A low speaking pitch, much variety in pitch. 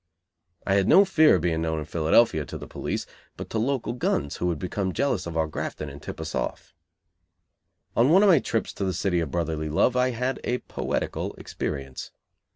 Yes: very low, 95 Hz; wide, 7.9 semitones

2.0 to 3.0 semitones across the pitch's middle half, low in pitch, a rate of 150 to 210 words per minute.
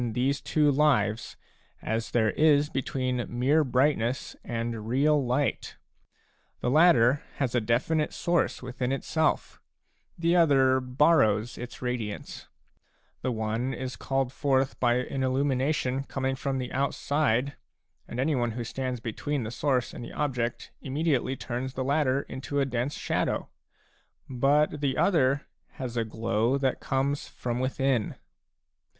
No: average, 2.7 semitones; low, 130 Hz; slow, 135 wpm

